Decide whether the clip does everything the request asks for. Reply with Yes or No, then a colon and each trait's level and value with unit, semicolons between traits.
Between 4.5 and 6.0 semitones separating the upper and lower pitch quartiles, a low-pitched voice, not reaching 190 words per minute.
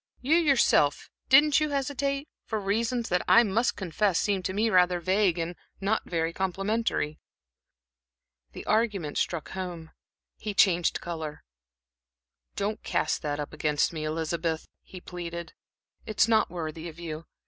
No: average, 5.0 semitones; medium, 185 Hz; average, 140 wpm